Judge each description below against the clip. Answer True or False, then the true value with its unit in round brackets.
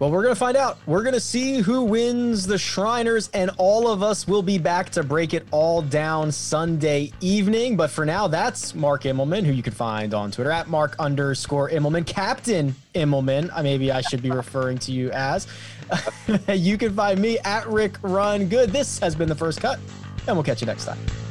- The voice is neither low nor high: True (165 Hz)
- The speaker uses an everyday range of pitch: False (6.9 semitones)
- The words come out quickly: True (210 wpm)